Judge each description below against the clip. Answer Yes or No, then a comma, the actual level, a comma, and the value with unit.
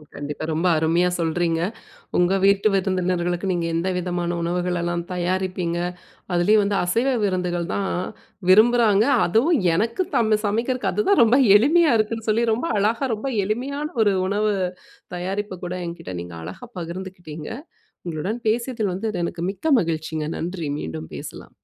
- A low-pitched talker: No, medium, 185 Hz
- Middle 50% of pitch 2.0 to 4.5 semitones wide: Yes, average, 4.0 semitones